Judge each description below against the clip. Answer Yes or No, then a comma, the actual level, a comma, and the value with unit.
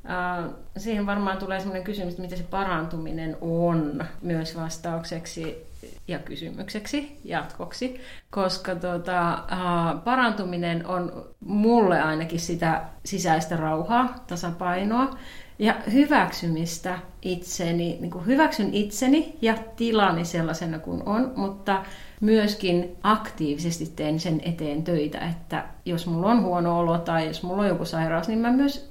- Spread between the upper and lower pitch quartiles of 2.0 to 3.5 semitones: No, average, 3.9 semitones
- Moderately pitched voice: Yes, medium, 180 Hz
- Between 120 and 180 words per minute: Yes, average, 125 wpm